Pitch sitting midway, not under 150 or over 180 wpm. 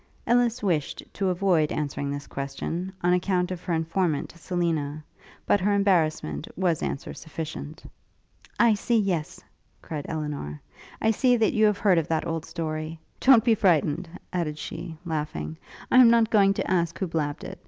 Yes: medium, 170 Hz; average, 165 wpm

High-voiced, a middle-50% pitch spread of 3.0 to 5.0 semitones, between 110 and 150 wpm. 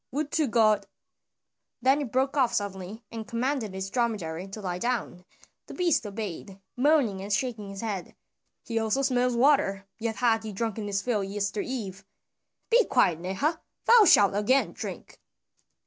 No: high, 220 Hz; average, 4.5 semitones; average, 160 wpm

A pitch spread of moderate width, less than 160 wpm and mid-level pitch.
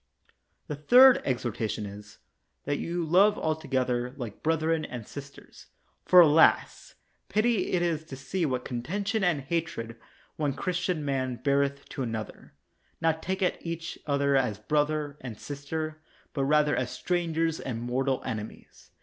Yes: average, 4.3 semitones; average, 150 wpm; medium, 145 Hz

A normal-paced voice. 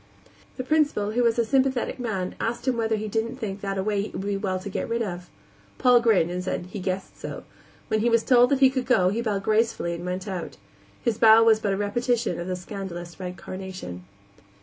No: fast, 230 wpm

